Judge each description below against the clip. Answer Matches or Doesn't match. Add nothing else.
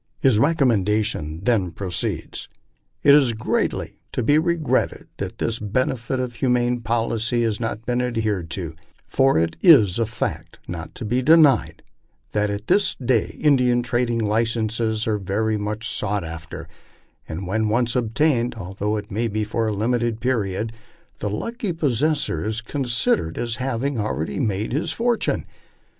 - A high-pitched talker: Doesn't match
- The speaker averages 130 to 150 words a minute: Doesn't match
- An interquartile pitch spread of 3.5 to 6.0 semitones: Doesn't match